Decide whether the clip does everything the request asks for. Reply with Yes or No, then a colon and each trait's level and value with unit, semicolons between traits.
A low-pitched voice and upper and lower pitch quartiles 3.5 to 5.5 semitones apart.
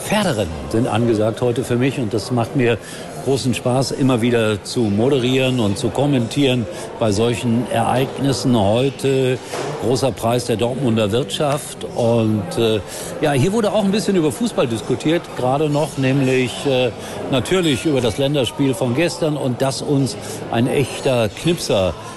No: low, 125 Hz; average, 2.9 semitones